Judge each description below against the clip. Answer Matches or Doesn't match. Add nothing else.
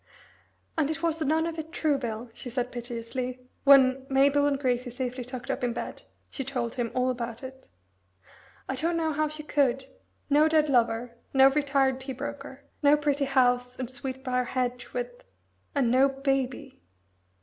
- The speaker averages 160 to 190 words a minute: Matches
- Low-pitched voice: Doesn't match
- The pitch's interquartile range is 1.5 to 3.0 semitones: Matches